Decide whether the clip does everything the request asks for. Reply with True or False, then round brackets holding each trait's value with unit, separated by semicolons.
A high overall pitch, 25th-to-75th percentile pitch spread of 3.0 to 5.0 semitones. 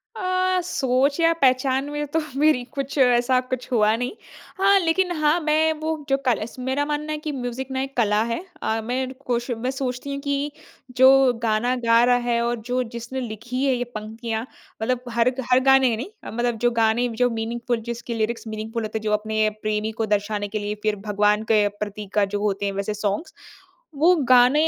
True (245 Hz; 3.6 semitones)